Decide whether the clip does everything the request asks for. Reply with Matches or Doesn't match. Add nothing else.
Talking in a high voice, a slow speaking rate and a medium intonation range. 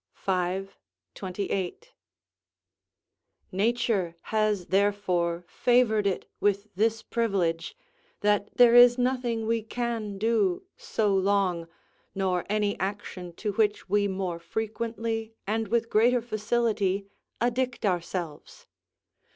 Matches